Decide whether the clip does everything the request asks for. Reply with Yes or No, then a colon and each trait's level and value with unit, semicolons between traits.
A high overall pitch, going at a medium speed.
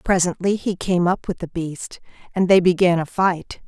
No: medium, 180 Hz; average, 195 wpm